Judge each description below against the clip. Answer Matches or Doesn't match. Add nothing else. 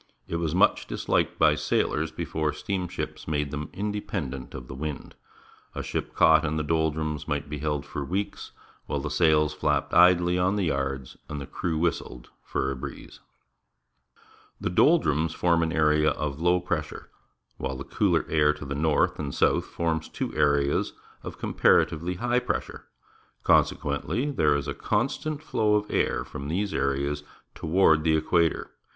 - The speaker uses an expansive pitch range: Doesn't match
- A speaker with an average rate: Matches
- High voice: Doesn't match